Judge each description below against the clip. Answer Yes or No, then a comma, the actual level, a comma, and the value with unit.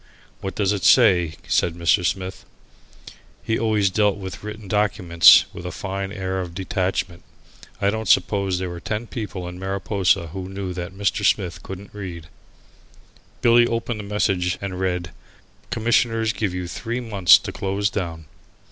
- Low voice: Yes, very low, 95 Hz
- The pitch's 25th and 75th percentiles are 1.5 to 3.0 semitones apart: Yes, average, 2.7 semitones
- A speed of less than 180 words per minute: Yes, average, 155 wpm